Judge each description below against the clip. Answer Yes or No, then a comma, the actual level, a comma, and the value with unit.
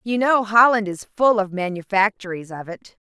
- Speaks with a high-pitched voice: Yes, high, 205 Hz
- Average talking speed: Yes, average, 175 wpm